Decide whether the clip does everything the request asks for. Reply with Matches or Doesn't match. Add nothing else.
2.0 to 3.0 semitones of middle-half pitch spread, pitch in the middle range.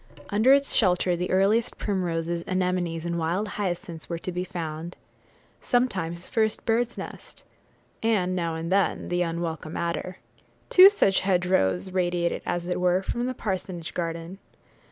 Matches